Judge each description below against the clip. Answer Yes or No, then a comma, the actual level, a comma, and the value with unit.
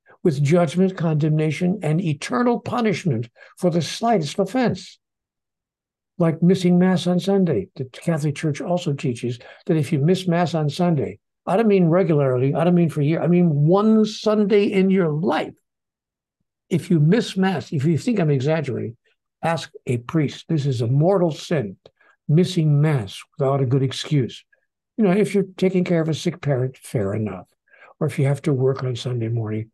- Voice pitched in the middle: Yes, medium, 165 Hz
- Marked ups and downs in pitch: No, average, 4.8 semitones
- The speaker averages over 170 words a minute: Yes, average, 180 wpm